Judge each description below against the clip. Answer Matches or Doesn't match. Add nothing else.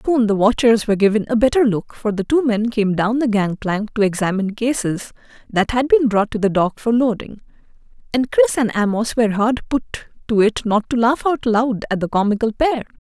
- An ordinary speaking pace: Doesn't match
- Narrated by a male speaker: Doesn't match